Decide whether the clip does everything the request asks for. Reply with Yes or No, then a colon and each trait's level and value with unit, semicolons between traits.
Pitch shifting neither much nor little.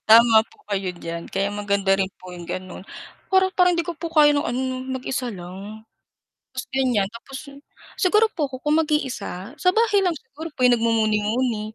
No: wide, 7.1 semitones